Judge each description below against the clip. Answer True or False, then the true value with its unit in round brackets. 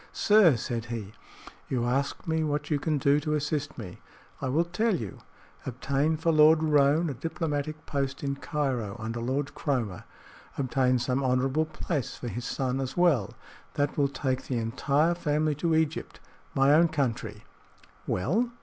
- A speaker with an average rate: True (160 wpm)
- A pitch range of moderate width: True (3.4 semitones)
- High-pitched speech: False (140 Hz)